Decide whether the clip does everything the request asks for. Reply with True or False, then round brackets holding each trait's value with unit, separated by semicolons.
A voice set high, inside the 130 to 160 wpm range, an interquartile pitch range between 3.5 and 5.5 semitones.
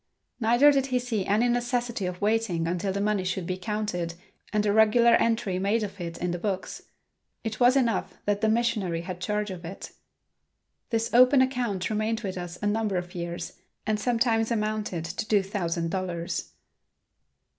False (210 Hz; 175 wpm; 4.0 semitones)